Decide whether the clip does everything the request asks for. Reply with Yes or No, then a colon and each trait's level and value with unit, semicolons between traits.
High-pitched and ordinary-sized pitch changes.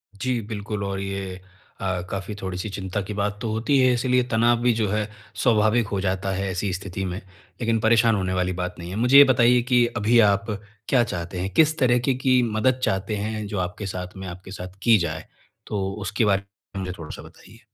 No: low, 100 Hz; average, 3.7 semitones